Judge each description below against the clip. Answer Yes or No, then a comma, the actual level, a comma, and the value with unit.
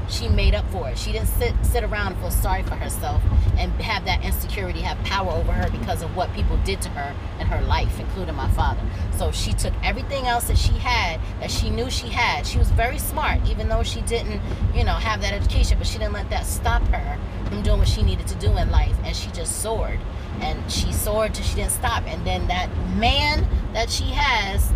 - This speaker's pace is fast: Yes, fast, 235 wpm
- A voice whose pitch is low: Yes, very low, 90 Hz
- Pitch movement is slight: Yes, narrow, 1.8 semitones